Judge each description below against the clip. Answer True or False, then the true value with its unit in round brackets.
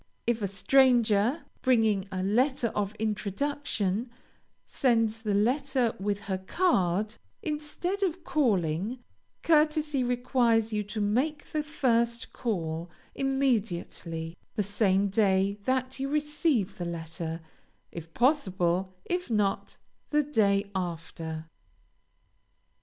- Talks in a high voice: True (220 Hz)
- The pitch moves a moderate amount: False (5.8 semitones)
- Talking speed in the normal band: False (110 wpm)